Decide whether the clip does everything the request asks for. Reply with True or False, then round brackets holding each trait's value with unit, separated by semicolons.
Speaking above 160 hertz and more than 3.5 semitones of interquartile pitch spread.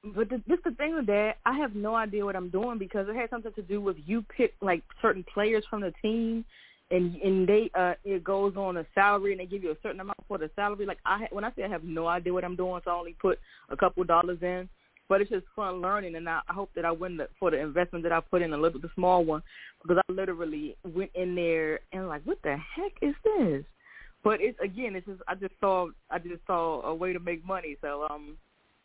False (190 Hz; 3.2 semitones)